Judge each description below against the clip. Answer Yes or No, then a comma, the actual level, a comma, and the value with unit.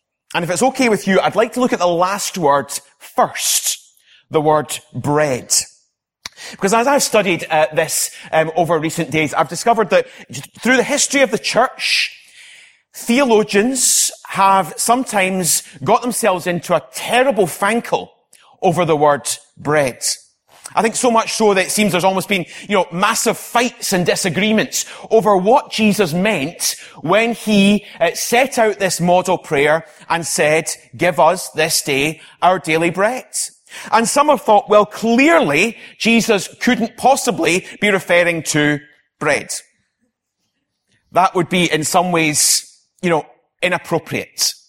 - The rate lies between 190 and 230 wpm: No, average, 145 wpm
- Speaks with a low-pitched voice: No, high, 190 Hz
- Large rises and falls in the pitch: Yes, wide, 5.8 semitones